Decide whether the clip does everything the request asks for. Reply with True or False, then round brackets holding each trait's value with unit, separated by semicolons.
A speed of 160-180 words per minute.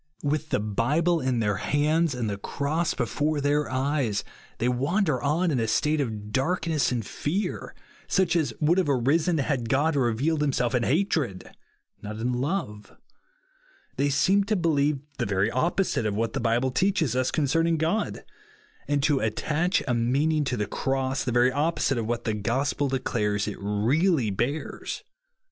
True (165 wpm)